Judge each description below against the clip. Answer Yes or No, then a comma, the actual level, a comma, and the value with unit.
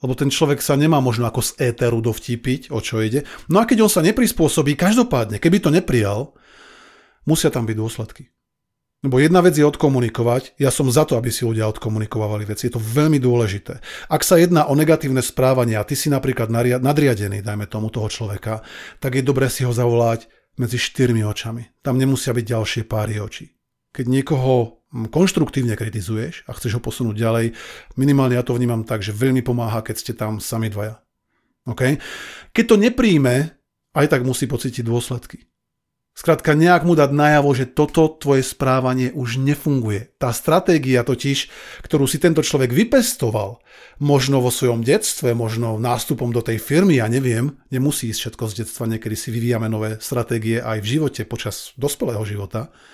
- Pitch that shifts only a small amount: No, average, 4.1 semitones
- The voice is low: Yes, low, 125 Hz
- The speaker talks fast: Yes, fast, 175 wpm